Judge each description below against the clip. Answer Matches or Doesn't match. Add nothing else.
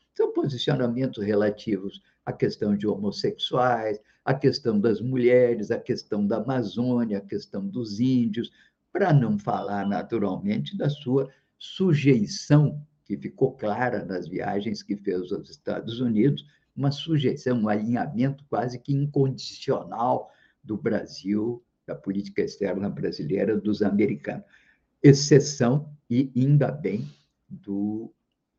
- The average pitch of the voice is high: Doesn't match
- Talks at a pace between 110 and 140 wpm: Matches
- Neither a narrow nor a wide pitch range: Matches